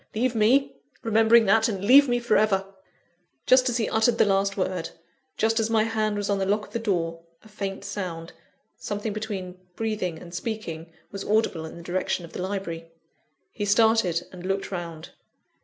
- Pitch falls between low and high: No, high, 205 Hz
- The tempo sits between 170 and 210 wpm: Yes, average, 185 wpm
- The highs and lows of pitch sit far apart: No, average, 3.5 semitones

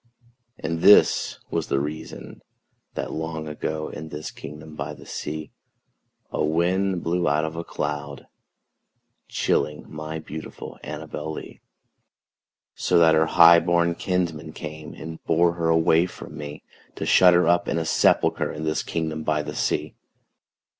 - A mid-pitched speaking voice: No, very low, 80 Hz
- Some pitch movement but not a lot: No, narrow, 1.6 semitones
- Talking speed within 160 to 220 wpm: No, average, 145 wpm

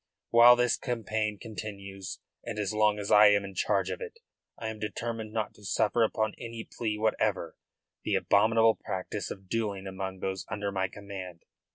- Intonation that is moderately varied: No, narrow, 2.3 semitones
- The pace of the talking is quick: No, average, 175 wpm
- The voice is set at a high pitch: No, low, 105 Hz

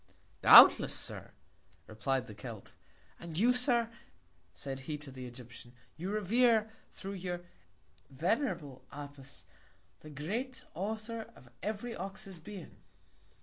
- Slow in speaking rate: Yes, slow, 115 wpm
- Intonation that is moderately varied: No, wide, 8.3 semitones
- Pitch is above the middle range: No, medium, 175 Hz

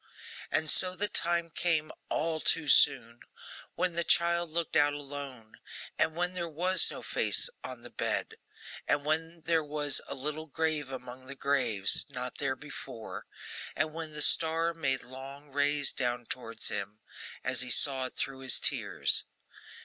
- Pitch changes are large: No, average, 3.7 semitones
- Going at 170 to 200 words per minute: No, average, 160 wpm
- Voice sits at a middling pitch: Yes, medium, 145 Hz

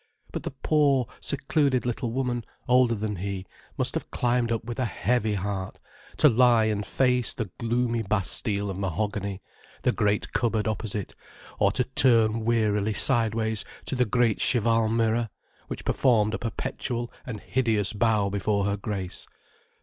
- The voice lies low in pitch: Yes, low, 115 Hz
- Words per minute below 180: Yes, average, 150 wpm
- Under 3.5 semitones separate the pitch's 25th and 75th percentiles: Yes, average, 2.9 semitones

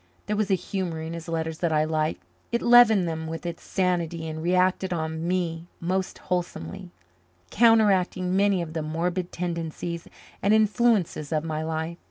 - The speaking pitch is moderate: Yes, medium, 175 Hz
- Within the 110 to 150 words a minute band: No, average, 165 wpm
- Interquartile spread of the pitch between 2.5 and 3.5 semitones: Yes, average, 2.8 semitones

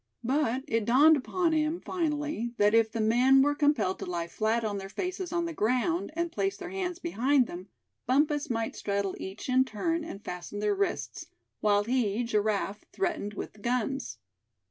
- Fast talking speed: No, average, 180 wpm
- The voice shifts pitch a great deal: Yes, wide, 6.7 semitones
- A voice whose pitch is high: Yes, high, 245 Hz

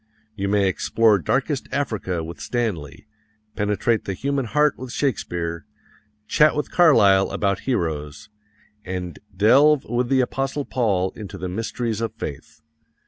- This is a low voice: Yes, low, 110 Hz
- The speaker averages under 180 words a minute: Yes, slow, 135 wpm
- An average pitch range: No, wide, 5.9 semitones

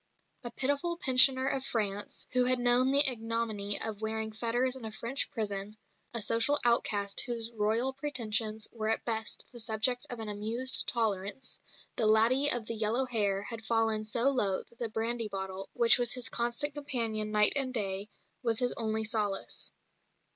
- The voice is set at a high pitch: Yes, high, 230 Hz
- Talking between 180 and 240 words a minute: No, average, 170 wpm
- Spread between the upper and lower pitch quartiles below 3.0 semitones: Yes, narrow, 2.5 semitones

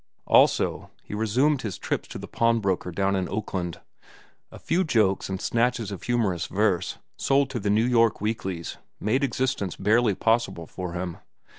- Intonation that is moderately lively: Yes, average, 4.1 semitones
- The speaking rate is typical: Yes, average, 165 wpm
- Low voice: Yes, low, 105 Hz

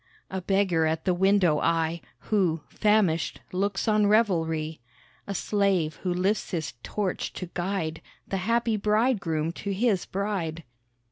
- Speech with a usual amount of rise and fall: Yes, average, 3.8 semitones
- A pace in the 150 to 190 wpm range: No, slow, 135 wpm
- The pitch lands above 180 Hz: Yes, high, 190 Hz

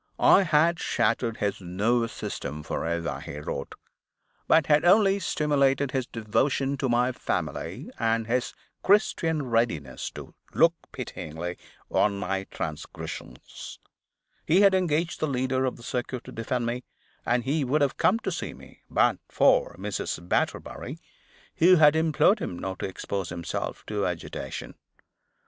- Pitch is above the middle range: No, low, 125 Hz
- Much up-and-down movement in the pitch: Yes, wide, 7.3 semitones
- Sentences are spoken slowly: No, average, 145 wpm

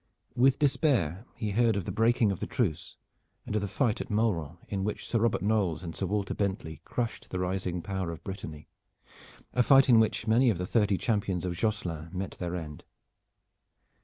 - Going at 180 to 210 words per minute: Yes, average, 190 wpm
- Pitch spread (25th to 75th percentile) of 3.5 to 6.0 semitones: Yes, average, 4.3 semitones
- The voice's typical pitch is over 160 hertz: No, low, 100 Hz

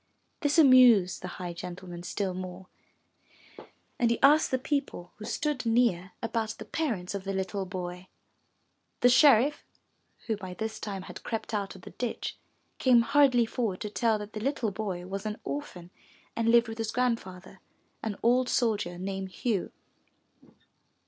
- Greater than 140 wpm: Yes, average, 160 wpm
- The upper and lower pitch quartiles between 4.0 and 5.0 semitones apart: Yes, average, 4.7 semitones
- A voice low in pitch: No, high, 215 Hz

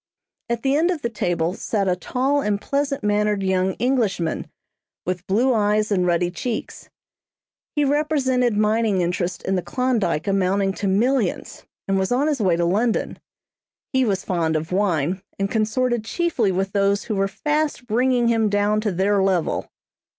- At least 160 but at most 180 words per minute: Yes, average, 165 wpm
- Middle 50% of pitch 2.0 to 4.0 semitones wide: No, average, 4.6 semitones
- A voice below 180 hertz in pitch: No, high, 210 Hz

